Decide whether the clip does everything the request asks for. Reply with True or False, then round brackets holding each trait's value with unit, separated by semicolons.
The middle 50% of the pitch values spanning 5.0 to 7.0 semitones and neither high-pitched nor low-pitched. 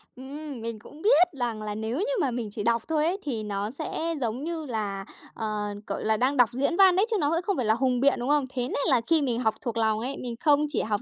False (5.4 semitones; 250 Hz)